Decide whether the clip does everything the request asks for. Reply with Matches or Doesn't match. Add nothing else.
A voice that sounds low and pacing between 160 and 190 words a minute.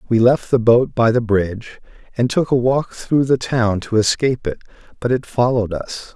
Doesn't match